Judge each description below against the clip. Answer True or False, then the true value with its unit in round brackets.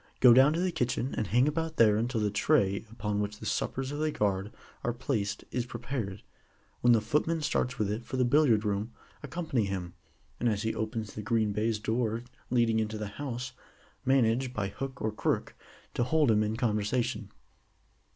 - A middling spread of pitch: True (3.7 semitones)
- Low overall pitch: True (115 Hz)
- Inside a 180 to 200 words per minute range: True (190 wpm)